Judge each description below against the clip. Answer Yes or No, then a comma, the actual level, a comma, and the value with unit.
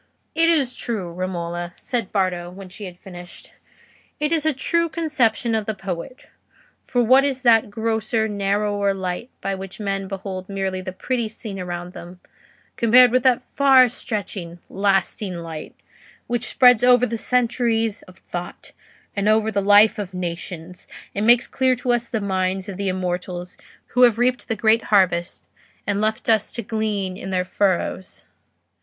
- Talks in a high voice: Yes, high, 205 Hz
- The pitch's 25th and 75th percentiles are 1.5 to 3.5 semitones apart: No, average, 4.3 semitones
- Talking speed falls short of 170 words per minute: Yes, average, 160 wpm